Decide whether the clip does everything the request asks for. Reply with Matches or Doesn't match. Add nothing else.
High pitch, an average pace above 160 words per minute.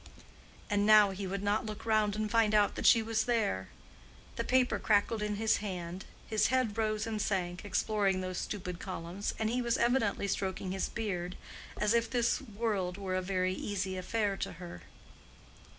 Matches